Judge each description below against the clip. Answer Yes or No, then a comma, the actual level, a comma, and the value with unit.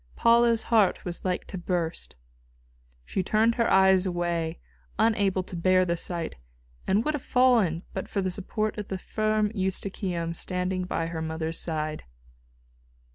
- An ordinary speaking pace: Yes, average, 150 wpm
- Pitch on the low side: No, medium, 185 Hz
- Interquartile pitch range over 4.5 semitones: No, average, 3.8 semitones